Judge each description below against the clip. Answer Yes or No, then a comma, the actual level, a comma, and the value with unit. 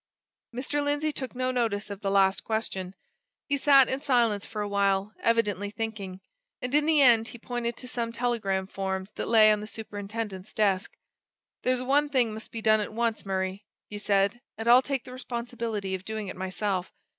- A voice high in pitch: Yes, high, 220 Hz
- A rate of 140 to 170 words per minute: No, average, 190 wpm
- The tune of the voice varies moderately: Yes, average, 3.6 semitones